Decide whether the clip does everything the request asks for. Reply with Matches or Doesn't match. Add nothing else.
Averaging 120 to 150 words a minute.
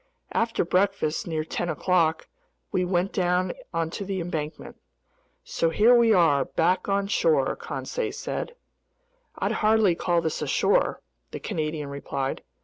Matches